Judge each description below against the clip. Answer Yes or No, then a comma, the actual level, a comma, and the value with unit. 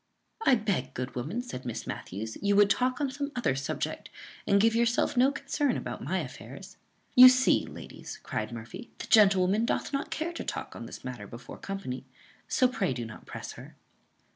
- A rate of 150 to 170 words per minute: No, average, 190 wpm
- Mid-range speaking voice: No, high, 205 Hz